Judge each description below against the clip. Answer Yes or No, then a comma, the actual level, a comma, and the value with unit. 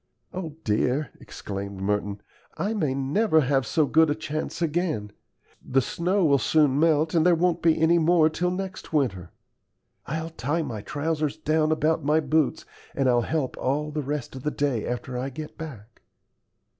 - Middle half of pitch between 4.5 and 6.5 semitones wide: No, average, 3.6 semitones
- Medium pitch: Yes, medium, 150 Hz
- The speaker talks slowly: No, average, 170 wpm